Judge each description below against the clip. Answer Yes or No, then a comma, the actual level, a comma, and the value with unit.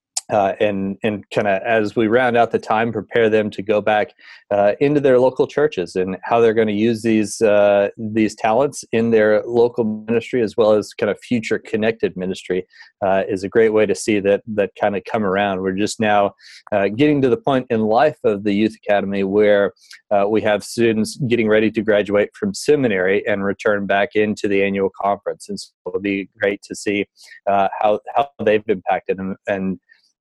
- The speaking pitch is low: Yes, low, 105 Hz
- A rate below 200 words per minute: No, fast, 205 wpm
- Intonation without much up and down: Yes, narrow, 2.2 semitones